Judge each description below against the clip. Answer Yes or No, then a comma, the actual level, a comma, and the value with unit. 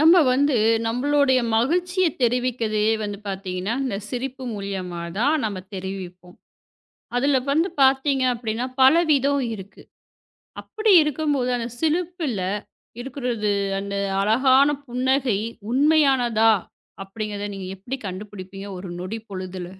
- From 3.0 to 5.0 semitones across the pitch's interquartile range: No, wide, 5.6 semitones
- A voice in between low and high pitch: No, high, 240 Hz